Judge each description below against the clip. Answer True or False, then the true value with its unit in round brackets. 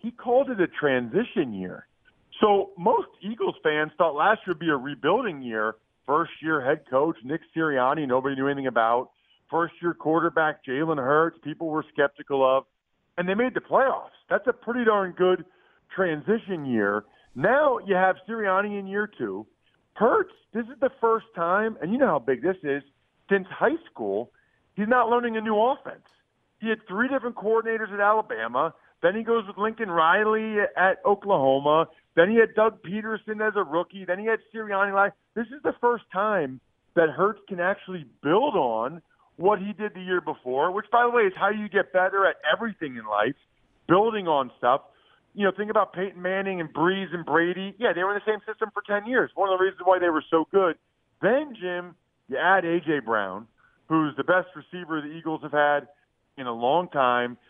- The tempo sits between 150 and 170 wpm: False (195 wpm)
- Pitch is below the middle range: False (185 Hz)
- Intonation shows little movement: False (5.6 semitones)